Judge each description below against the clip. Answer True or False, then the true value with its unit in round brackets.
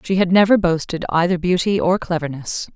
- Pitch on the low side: False (175 Hz)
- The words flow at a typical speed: True (175 wpm)